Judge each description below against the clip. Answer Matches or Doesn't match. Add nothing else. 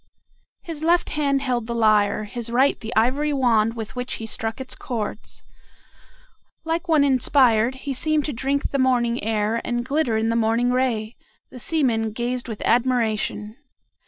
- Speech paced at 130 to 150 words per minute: Doesn't match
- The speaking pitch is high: Matches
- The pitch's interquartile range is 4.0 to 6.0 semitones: Doesn't match